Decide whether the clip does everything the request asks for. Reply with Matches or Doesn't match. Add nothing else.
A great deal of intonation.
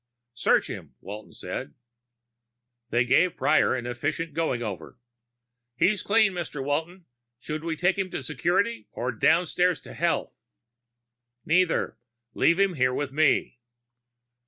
Matches